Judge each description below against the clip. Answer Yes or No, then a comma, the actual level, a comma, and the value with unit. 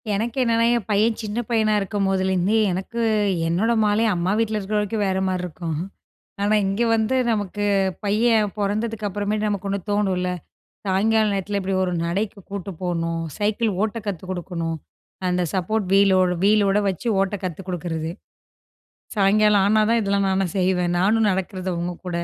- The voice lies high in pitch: Yes, high, 200 Hz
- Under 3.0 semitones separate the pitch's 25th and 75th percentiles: Yes, narrow, 2.6 semitones